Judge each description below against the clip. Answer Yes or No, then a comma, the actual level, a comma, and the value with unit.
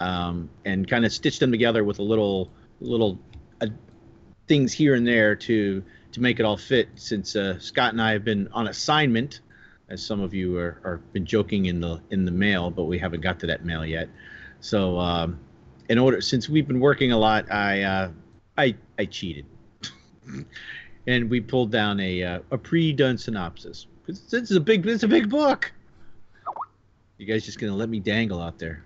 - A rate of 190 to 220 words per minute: Yes, average, 200 wpm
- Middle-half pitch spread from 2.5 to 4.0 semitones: No, average, 4.8 semitones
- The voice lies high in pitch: No, low, 105 Hz